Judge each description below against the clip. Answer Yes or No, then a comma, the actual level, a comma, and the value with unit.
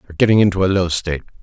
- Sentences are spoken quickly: Yes, fast, 250 wpm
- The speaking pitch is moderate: No, very low, 90 Hz